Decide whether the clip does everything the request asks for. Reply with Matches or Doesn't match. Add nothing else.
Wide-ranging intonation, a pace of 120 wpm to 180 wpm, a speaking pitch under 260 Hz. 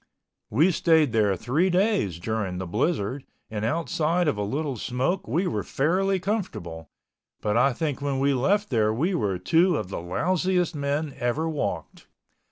Matches